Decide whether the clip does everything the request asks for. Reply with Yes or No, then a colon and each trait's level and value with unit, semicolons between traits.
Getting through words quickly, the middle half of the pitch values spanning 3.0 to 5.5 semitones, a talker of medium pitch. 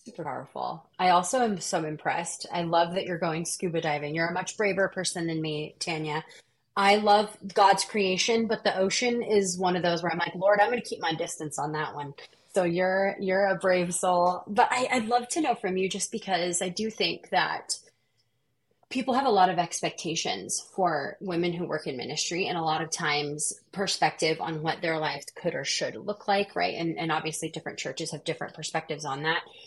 Yes: fast, 210 wpm; average, 3.7 semitones; medium, 180 Hz